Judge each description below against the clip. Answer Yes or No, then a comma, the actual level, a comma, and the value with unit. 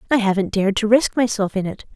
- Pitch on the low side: No, high, 210 Hz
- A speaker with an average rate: No, fast, 245 wpm